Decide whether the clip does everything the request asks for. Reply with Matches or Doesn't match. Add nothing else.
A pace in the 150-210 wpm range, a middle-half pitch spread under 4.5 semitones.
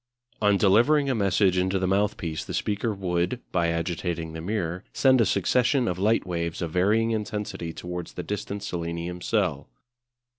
Matches